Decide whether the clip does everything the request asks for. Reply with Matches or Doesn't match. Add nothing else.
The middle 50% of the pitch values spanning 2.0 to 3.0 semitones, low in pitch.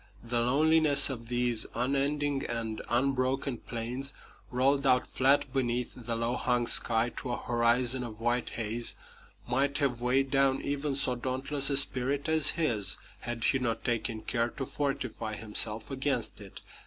Matches